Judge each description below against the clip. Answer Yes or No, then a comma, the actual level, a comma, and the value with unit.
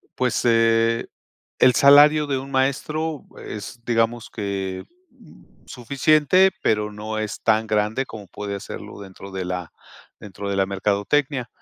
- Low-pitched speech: Yes, low, 115 Hz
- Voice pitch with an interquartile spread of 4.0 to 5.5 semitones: Yes, average, 4.8 semitones